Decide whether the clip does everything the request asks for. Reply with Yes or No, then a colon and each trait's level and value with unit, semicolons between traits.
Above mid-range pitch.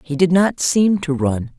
No: medium, 165 Hz